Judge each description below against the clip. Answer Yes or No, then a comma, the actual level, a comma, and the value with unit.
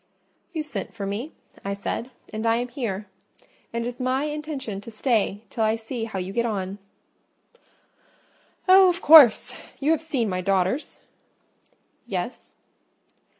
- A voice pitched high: Yes, high, 230 Hz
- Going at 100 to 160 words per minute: Yes, average, 150 wpm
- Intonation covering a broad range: Yes, wide, 5.7 semitones